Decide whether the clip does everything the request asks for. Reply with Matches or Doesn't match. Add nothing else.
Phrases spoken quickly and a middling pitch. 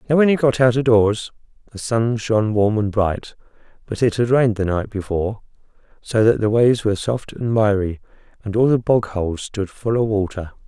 Doesn't match